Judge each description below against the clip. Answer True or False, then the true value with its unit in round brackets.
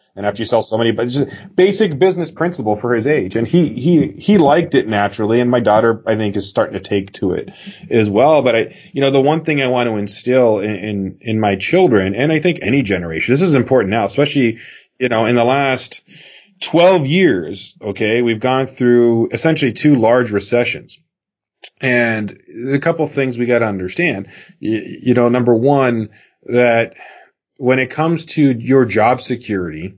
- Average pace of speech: True (195 wpm)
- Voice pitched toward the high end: False (125 Hz)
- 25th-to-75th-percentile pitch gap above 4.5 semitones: True (4.9 semitones)